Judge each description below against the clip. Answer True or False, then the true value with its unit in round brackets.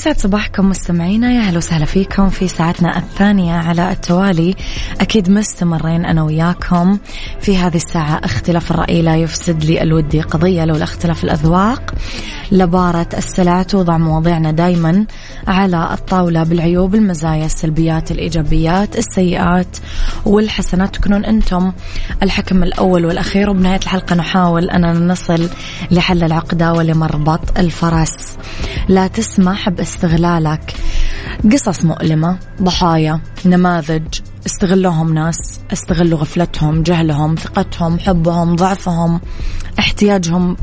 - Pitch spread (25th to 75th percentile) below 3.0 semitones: True (2.4 semitones)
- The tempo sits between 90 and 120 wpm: True (105 wpm)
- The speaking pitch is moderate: True (175 Hz)